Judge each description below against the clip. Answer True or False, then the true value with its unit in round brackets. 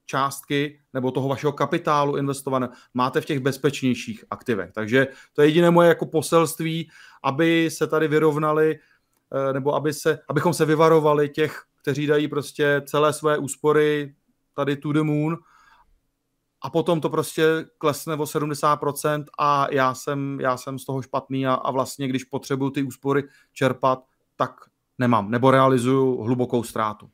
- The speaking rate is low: False (150 wpm)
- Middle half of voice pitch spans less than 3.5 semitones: True (2.4 semitones)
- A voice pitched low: False (145 Hz)